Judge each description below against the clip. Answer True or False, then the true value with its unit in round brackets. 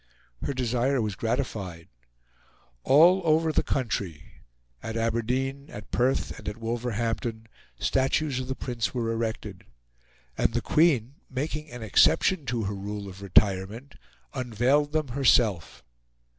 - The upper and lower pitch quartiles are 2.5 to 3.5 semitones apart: False (3.9 semitones)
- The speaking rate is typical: False (130 wpm)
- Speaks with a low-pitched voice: True (120 Hz)